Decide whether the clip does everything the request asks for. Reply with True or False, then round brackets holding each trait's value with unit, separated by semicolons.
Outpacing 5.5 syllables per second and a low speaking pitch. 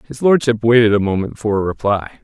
True (6.2 syllables/s; 110 Hz)